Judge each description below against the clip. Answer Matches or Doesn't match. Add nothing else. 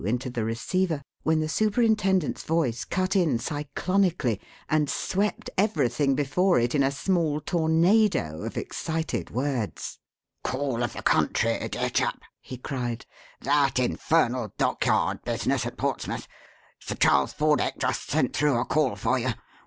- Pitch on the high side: Doesn't match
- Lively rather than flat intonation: Matches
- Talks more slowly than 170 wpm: Matches